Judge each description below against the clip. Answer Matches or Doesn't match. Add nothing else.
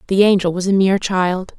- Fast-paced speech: Matches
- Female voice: Matches